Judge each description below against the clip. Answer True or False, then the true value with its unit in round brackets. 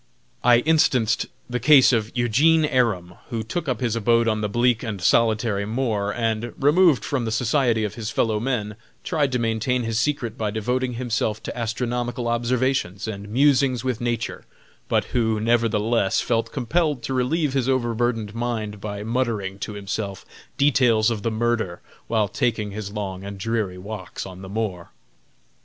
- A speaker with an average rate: True (165 wpm)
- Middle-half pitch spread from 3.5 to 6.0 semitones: False (2.8 semitones)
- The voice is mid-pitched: False (115 Hz)